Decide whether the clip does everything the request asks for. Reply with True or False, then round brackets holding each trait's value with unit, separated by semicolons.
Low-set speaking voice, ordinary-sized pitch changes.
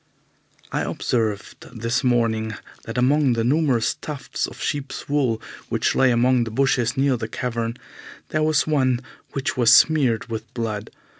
True (125 Hz; 3.2 semitones)